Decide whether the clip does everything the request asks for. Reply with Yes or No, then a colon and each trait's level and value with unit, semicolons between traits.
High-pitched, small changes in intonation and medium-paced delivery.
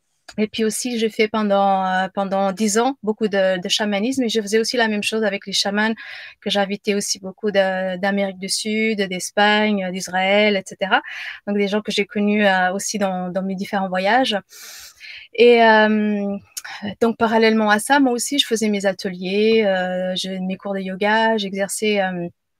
Yes: high, 205 Hz; narrow, 2.1 semitones; average, 180 wpm